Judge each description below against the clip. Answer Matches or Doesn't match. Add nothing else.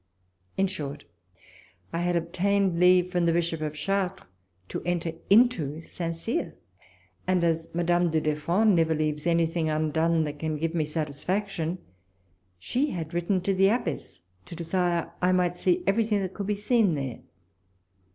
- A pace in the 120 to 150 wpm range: Doesn't match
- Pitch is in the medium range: Matches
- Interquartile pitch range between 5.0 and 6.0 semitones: Doesn't match